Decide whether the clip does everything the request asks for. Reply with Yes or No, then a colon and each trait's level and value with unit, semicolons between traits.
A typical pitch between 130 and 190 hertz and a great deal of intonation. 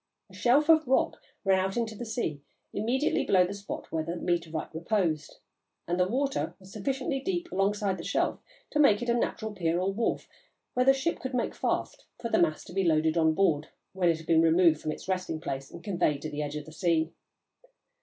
Yes: medium, 185 Hz; wide, 6.3 semitones